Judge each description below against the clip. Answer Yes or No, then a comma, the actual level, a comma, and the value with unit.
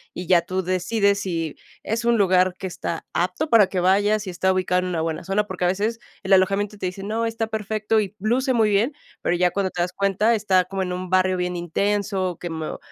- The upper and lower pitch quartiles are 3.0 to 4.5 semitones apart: No, narrow, 2.6 semitones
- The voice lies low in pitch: No, high, 190 Hz